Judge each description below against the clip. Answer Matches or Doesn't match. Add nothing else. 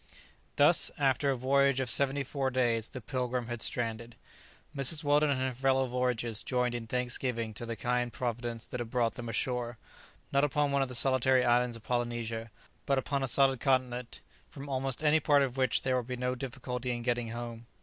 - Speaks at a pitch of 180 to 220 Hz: Doesn't match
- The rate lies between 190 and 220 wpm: Matches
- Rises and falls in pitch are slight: Matches